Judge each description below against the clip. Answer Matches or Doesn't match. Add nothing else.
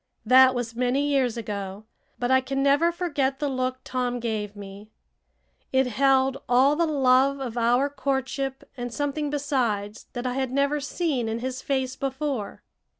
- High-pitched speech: Matches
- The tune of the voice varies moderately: Doesn't match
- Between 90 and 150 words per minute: Doesn't match